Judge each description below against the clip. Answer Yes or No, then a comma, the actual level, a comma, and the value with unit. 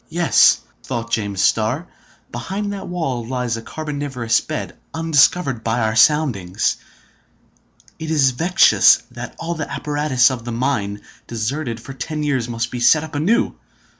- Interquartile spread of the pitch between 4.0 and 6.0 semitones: Yes, average, 5.2 semitones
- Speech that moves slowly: No, average, 145 wpm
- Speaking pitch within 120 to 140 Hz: Yes, low, 135 Hz